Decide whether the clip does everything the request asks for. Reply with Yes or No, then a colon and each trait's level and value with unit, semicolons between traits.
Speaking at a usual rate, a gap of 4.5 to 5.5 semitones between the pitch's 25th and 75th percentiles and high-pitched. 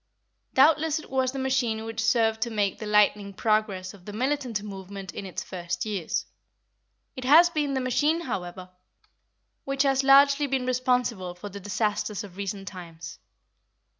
Yes: average, 160 wpm; average, 5.2 semitones; high, 220 Hz